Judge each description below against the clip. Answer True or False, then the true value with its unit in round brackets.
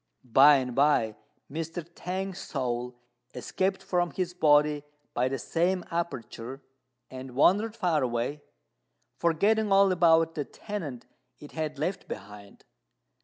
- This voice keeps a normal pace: False (120 wpm)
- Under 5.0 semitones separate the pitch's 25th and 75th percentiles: False (5.6 semitones)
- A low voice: False (155 Hz)